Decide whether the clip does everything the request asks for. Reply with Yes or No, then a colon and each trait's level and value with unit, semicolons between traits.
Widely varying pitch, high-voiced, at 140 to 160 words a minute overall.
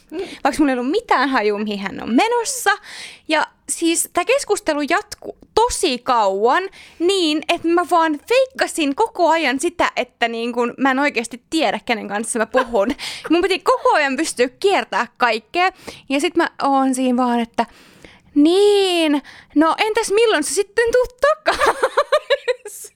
Yes: wide, 7.2 semitones; very high, 320 Hz; average, 150 wpm